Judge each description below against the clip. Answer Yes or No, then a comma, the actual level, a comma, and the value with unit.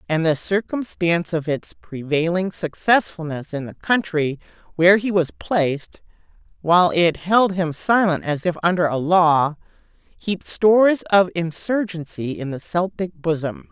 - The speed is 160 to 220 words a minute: No, average, 140 wpm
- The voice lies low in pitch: No, medium, 175 Hz